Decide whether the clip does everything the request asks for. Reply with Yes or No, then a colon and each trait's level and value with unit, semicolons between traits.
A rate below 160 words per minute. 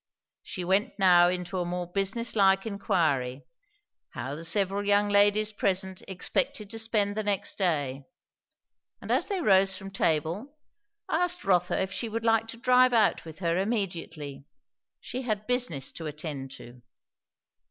Yes: average, 150 wpm